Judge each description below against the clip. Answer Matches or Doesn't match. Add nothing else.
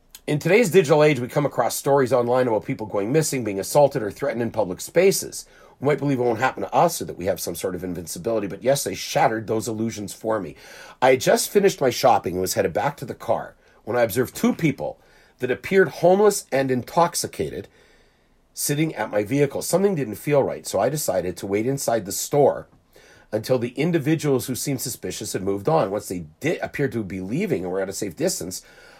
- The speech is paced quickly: Matches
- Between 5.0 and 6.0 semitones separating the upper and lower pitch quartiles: Matches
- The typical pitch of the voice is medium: Doesn't match